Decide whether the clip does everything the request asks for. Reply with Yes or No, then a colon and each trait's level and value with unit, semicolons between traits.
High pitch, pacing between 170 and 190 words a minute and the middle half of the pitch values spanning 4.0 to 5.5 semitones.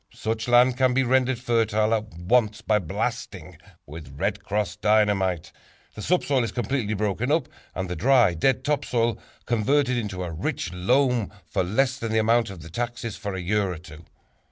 No: low, 110 Hz; average, 180 wpm; average, 4.4 semitones